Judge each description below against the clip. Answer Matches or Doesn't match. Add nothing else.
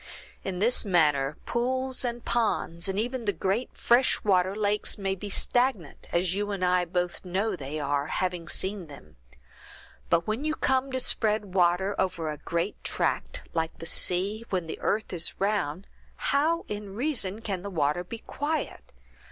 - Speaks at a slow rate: Doesn't match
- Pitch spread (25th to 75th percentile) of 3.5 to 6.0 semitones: Matches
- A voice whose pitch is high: Matches